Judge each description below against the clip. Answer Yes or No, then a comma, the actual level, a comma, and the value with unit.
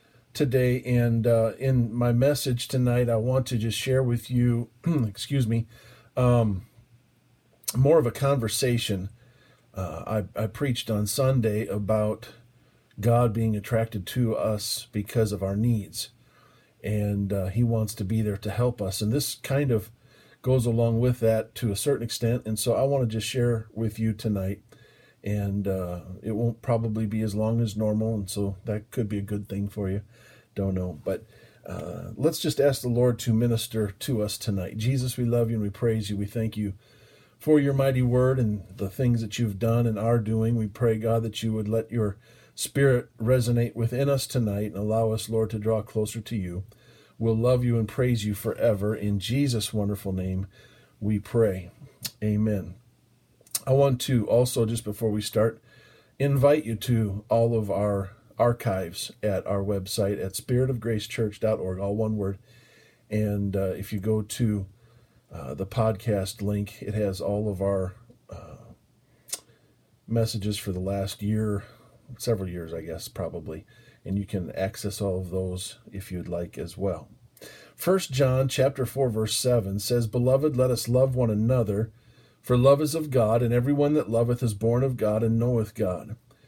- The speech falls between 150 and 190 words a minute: Yes, average, 175 wpm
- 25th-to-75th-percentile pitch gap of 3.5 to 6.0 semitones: No, average, 2.7 semitones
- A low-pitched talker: Yes, low, 115 Hz